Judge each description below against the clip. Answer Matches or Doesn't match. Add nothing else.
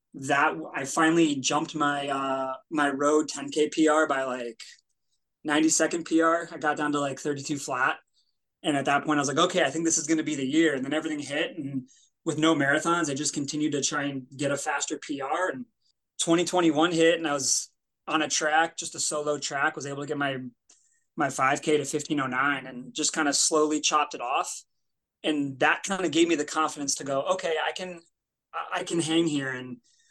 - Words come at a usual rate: Doesn't match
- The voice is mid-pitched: Matches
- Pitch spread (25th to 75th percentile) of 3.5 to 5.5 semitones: Doesn't match